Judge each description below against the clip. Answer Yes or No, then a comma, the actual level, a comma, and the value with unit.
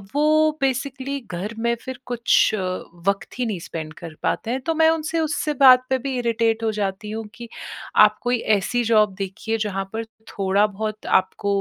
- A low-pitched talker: No, high, 230 Hz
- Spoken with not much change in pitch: No, average, 4.3 semitones